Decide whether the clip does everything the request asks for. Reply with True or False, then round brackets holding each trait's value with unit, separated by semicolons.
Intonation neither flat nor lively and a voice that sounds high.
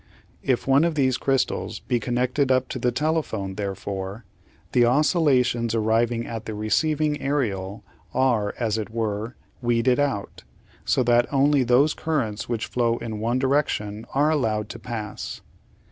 False (3.8 semitones; 120 Hz)